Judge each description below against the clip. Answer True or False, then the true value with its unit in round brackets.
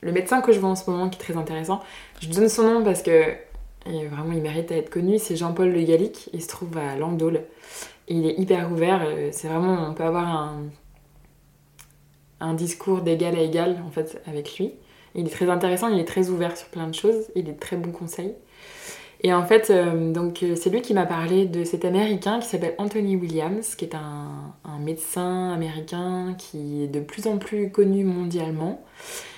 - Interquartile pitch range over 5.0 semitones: False (3.4 semitones)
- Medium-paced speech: True (200 wpm)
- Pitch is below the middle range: False (175 Hz)